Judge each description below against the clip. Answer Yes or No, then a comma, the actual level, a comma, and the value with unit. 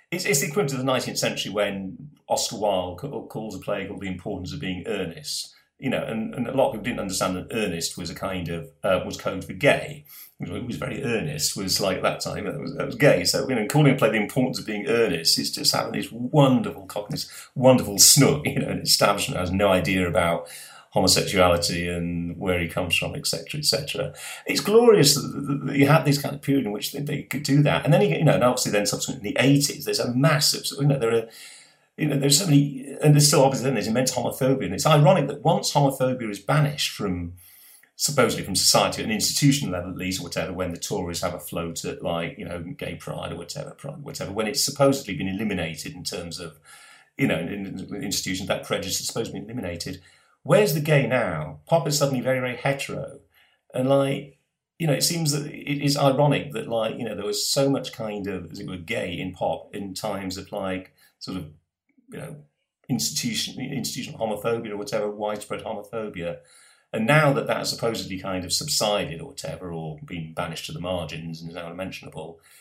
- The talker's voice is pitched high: No, low, 125 Hz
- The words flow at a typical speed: No, fast, 220 wpm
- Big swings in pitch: Yes, wide, 7.2 semitones